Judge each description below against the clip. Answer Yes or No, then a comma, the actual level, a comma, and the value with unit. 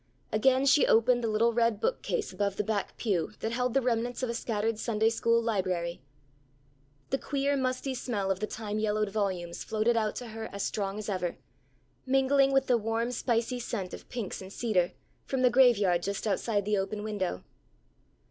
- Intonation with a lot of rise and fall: No, average, 3.4 semitones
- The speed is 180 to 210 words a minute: Yes, average, 185 wpm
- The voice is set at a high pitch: Yes, high, 225 Hz